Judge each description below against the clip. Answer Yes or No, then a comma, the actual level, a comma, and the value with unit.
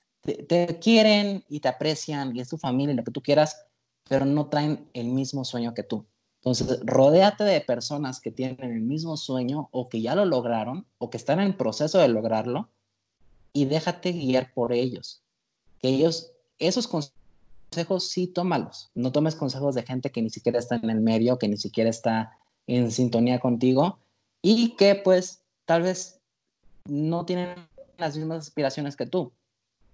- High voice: No, medium, 140 Hz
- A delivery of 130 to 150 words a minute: No, average, 170 wpm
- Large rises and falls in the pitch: Yes, wide, 6.0 semitones